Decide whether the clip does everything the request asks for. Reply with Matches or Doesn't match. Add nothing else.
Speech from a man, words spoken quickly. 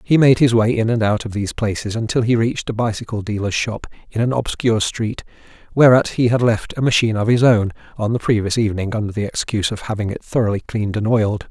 Matches